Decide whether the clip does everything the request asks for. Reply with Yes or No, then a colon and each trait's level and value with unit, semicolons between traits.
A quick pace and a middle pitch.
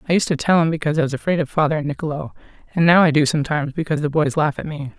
Yes: fast, 290 wpm; medium, 155 Hz